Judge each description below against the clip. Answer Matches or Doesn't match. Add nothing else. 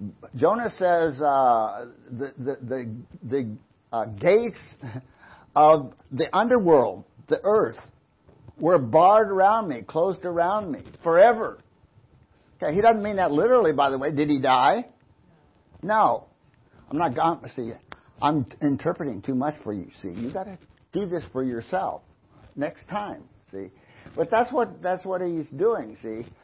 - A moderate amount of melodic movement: Doesn't match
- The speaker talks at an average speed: Matches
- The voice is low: Doesn't match